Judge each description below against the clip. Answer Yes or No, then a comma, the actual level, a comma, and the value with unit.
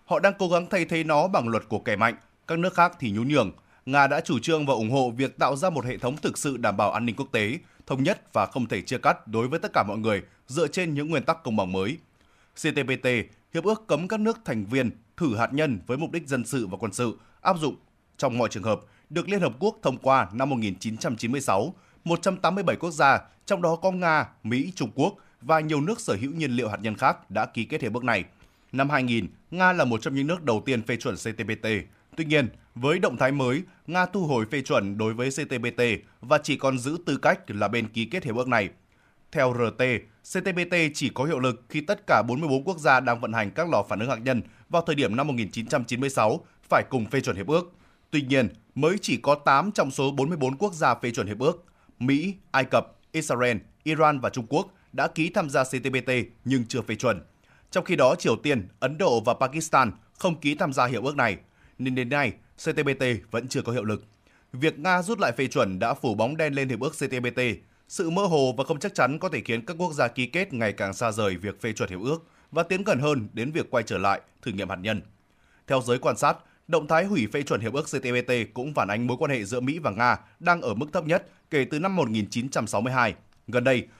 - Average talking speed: Yes, average, 240 wpm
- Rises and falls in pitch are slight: No, wide, 5.6 semitones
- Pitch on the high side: No, low, 135 Hz